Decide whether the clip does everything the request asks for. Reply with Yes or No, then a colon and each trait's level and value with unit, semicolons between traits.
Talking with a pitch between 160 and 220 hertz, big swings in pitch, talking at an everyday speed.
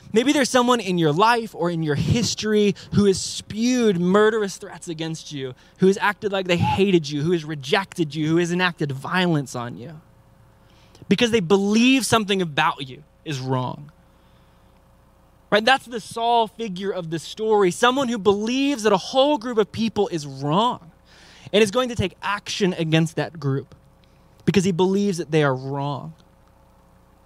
Yes: medium, 185 Hz; wide, 5.8 semitones; average, 170 wpm